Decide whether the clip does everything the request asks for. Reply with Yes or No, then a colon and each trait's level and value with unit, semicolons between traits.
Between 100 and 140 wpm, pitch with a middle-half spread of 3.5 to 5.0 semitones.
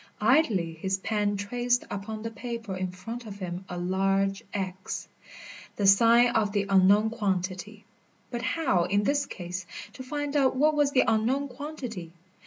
No: average, 160 wpm; average, 4.4 semitones